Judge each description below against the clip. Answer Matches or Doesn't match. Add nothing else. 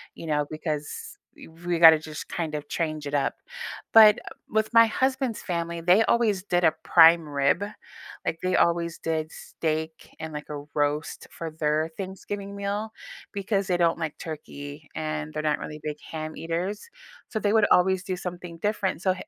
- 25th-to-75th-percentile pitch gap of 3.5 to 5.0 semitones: Matches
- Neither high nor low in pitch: Matches